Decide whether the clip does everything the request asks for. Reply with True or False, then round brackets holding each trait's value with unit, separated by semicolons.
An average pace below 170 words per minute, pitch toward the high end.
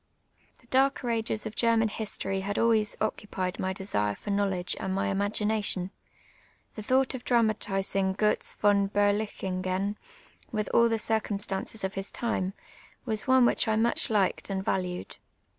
True (150 wpm; 205 Hz)